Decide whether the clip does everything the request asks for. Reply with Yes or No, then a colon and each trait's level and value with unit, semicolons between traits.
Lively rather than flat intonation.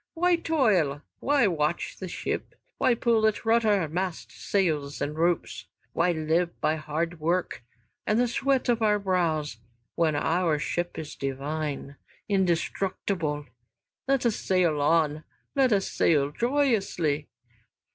Yes: wide, 5.9 semitones